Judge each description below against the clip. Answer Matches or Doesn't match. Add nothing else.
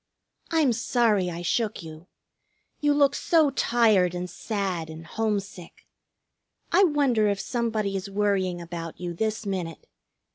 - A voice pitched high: Matches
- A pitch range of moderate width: Matches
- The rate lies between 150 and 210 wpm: Doesn't match